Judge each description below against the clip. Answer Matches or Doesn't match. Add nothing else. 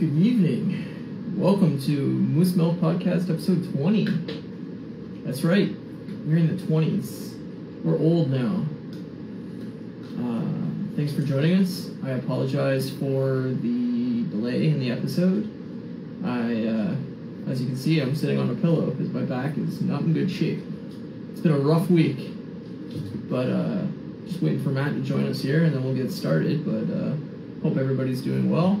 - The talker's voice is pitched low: Doesn't match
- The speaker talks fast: Doesn't match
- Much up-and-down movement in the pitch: Matches